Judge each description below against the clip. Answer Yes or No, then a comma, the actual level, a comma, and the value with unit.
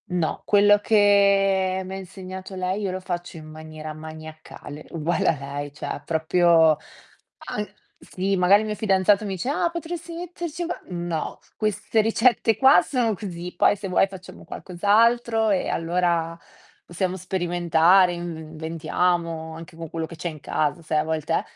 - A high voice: No, medium, 180 Hz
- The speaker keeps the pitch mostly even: No, average, 3.9 semitones